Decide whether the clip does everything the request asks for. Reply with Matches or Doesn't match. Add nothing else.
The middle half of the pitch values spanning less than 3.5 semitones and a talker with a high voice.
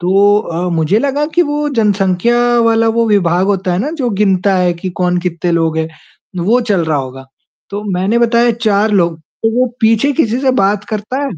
Doesn't match